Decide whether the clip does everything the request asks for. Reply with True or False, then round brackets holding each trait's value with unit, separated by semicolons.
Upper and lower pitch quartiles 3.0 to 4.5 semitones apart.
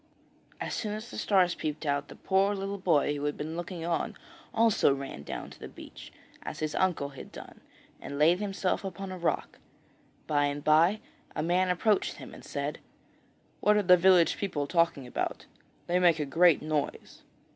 True (4.2 semitones)